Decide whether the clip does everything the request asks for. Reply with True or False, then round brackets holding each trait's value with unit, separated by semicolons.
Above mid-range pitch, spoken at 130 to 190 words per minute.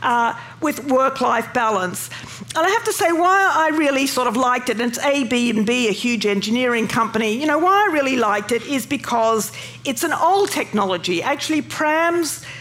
False (250 Hz; 200 wpm)